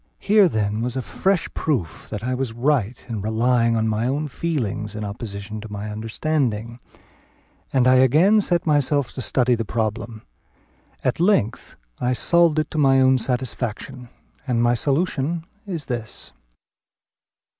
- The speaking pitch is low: Yes, low, 125 Hz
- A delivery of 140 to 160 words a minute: Yes, average, 150 wpm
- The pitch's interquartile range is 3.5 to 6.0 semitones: Yes, average, 4.7 semitones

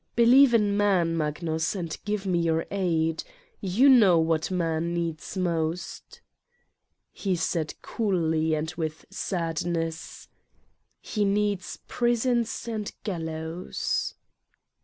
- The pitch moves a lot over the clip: No, average, 4.1 semitones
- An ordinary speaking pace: No, slow, 105 wpm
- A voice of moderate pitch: Yes, medium, 175 Hz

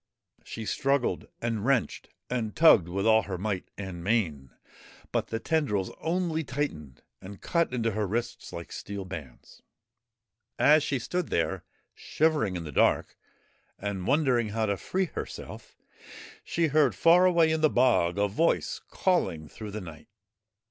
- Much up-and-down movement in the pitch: Yes, wide, 8.0 semitones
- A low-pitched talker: Yes, low, 115 Hz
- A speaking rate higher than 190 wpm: No, average, 150 wpm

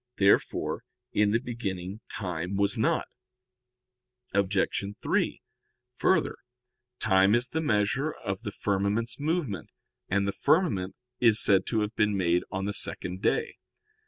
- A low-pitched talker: Yes, low, 100 Hz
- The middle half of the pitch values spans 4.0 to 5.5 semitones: No, average, 3.3 semitones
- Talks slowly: Yes, slow, 130 wpm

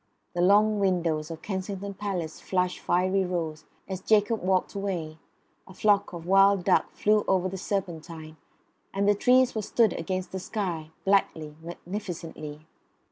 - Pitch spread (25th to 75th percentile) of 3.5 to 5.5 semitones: No, average, 3.1 semitones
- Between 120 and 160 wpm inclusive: Yes, average, 145 wpm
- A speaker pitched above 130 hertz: Yes, medium, 185 Hz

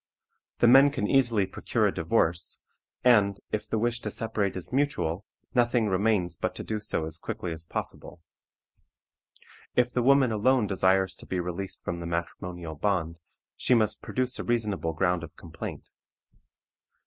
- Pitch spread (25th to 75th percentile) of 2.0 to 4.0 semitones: No, wide, 5.4 semitones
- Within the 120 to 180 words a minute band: Yes, average, 160 wpm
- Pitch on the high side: No, low, 100 Hz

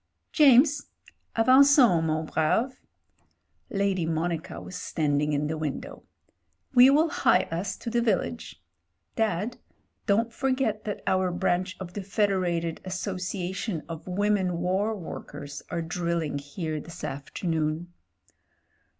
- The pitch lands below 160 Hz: No, medium, 185 Hz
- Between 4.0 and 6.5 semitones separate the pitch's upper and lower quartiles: Yes, average, 5.0 semitones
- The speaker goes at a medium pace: No, slow, 125 wpm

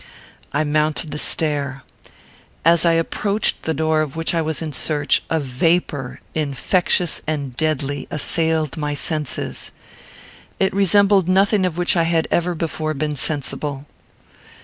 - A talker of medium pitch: Yes, medium, 155 Hz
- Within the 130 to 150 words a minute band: Yes, average, 140 wpm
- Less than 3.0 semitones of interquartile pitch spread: Yes, narrow, 2.5 semitones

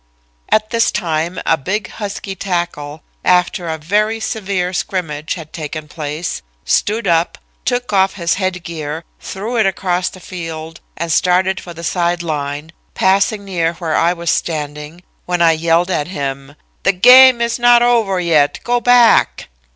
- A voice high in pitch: No, medium, 175 Hz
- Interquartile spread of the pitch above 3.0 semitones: Yes, average, 3.7 semitones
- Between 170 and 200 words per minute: No, average, 160 wpm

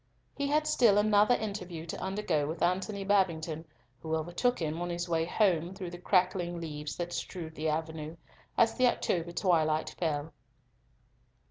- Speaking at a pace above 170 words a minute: No, average, 155 wpm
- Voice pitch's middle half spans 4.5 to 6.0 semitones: No, average, 3.8 semitones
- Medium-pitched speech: Yes, medium, 175 Hz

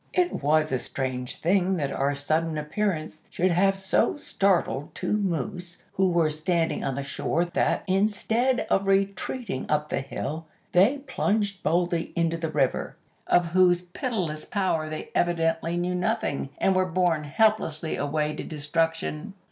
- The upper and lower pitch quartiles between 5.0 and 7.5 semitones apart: No, average, 3.8 semitones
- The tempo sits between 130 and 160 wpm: Yes, average, 150 wpm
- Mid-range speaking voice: Yes, medium, 170 Hz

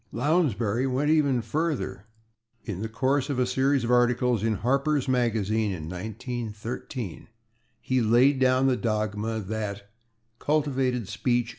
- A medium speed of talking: No, slow, 130 wpm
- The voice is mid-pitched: No, low, 120 Hz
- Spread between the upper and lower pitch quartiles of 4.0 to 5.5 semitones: No, average, 3.4 semitones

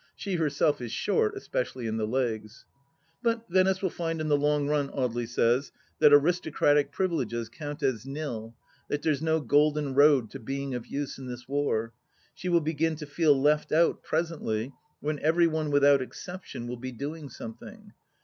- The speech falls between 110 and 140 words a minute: No, average, 175 wpm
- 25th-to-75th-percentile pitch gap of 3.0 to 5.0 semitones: Yes, average, 3.9 semitones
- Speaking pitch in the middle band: Yes, medium, 145 Hz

